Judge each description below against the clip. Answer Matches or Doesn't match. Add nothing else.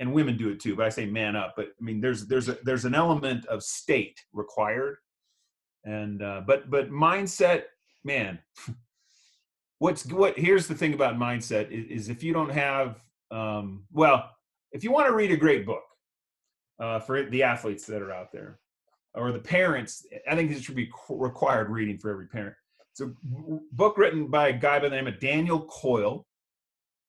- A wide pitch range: Matches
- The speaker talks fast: Doesn't match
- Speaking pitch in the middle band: Doesn't match